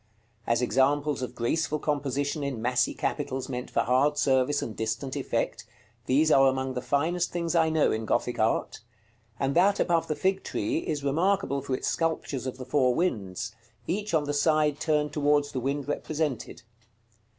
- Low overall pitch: No, medium, 145 Hz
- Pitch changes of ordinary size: Yes, average, 3.4 semitones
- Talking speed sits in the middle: Yes, average, 175 wpm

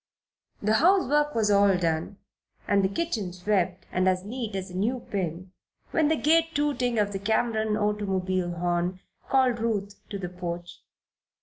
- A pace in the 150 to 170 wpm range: Yes, average, 160 wpm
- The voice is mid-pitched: No, high, 200 Hz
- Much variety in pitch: No, average, 4.4 semitones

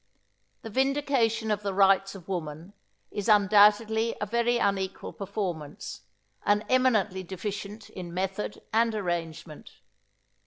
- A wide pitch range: No, average, 2.8 semitones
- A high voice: Yes, high, 205 Hz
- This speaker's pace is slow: Yes, slow, 115 wpm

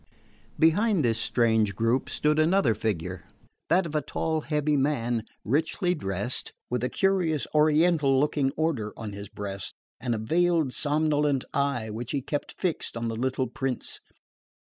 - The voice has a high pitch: No, medium, 140 Hz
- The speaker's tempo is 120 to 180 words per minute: Yes, average, 150 wpm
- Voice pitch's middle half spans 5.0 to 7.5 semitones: Yes, wide, 5.4 semitones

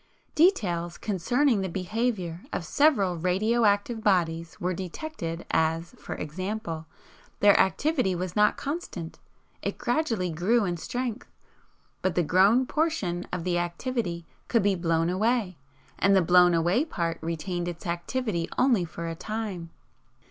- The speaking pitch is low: No, medium, 185 Hz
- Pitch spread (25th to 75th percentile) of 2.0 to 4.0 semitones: No, average, 4.9 semitones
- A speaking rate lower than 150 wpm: Yes, average, 140 wpm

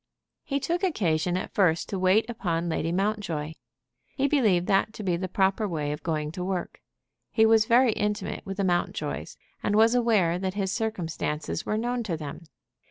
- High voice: Yes, high, 195 Hz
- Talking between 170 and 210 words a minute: Yes, average, 180 wpm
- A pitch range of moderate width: Yes, average, 4.6 semitones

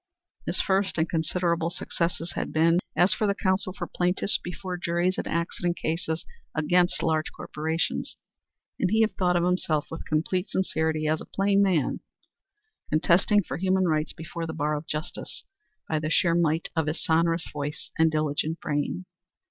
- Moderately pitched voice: Yes, medium, 170 Hz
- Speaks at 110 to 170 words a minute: Yes, average, 165 wpm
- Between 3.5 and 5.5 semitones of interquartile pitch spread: No, narrow, 2.4 semitones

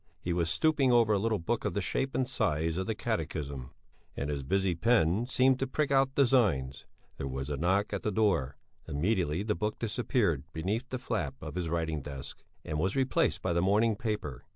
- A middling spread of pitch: No, wide, 6.6 semitones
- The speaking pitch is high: No, very low, 95 Hz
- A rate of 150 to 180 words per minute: No, average, 200 wpm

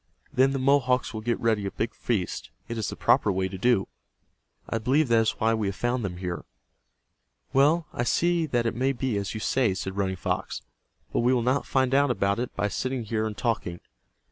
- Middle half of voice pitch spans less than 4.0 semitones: No, average, 4.3 semitones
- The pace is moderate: No, fast, 220 wpm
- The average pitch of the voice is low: Yes, low, 115 Hz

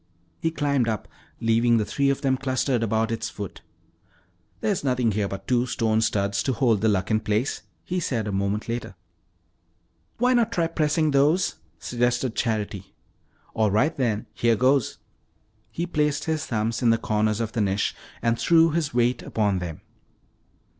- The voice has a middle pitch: No, low, 120 Hz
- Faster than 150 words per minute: Yes, average, 160 wpm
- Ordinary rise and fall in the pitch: Yes, average, 4.8 semitones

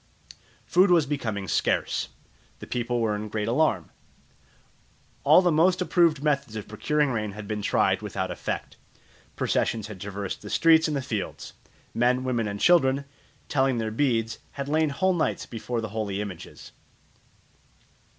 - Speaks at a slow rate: No, average, 150 wpm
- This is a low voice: Yes, low, 120 Hz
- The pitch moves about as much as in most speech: No, wide, 5.9 semitones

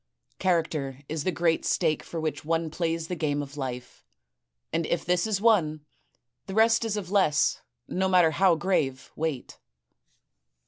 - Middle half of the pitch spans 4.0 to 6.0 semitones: No, average, 3.5 semitones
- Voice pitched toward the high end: No, medium, 165 Hz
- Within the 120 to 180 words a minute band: Yes, average, 155 wpm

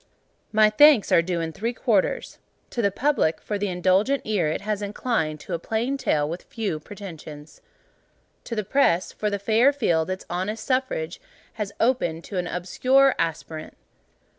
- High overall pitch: Yes, high, 200 Hz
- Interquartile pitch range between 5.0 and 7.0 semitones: Yes, average, 5.3 semitones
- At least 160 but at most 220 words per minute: Yes, average, 165 wpm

